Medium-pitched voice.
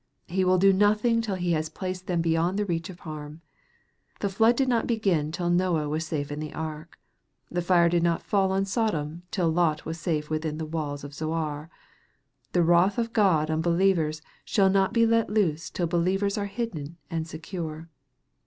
Yes: medium, 170 Hz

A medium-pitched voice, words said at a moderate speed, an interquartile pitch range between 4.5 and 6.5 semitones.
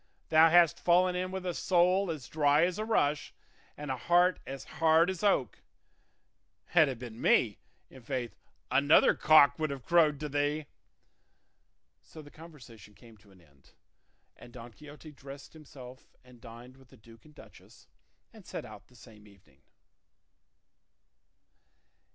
Yes: medium, 145 Hz; average, 150 wpm; average, 5.1 semitones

